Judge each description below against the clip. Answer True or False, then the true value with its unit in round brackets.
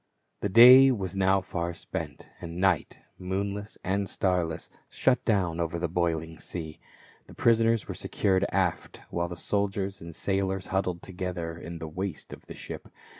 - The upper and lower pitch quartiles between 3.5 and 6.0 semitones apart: False (2.5 semitones)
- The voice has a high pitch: False (95 Hz)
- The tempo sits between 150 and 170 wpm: True (160 wpm)